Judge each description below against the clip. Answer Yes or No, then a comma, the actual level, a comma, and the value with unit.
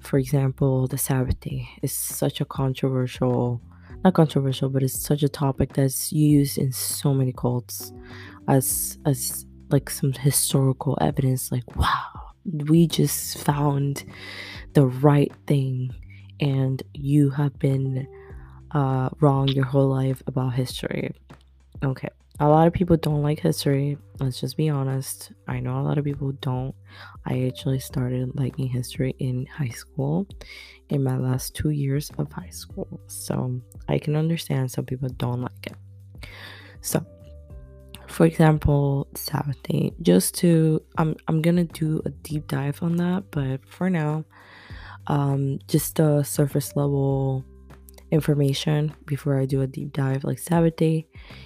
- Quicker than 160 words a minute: No, average, 145 wpm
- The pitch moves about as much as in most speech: No, wide, 6.0 semitones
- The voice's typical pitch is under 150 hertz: Yes, low, 135 Hz